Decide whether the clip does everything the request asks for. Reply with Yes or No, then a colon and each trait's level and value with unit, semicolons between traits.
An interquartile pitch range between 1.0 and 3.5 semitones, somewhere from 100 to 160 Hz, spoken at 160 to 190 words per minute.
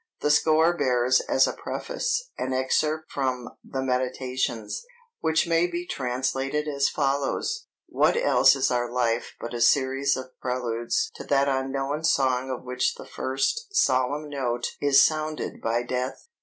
No: average, 3.1 semitones; low, 135 Hz; average, 150 wpm